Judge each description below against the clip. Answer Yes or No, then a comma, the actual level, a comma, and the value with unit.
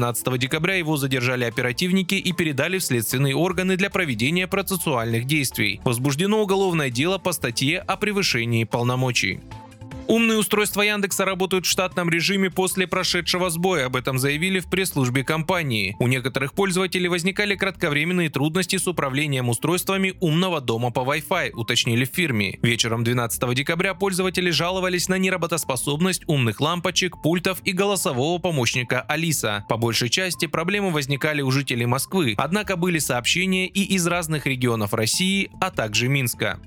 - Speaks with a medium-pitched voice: Yes, medium, 165 Hz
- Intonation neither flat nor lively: No, wide, 6.6 semitones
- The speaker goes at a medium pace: Yes, average, 140 wpm